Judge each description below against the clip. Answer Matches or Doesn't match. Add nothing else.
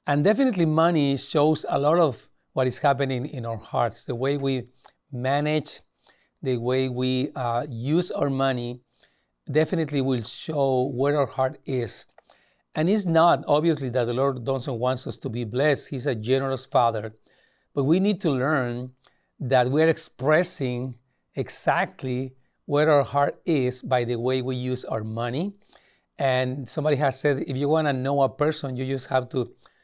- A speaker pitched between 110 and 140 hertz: Matches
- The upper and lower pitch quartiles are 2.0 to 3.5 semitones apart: Matches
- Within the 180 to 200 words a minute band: Doesn't match